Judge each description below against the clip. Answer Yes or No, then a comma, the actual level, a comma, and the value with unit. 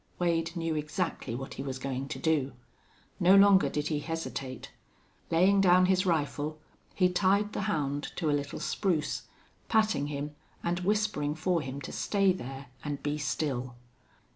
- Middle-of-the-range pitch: Yes, medium, 160 Hz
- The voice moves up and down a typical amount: Yes, average, 4.3 semitones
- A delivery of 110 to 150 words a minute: No, average, 160 wpm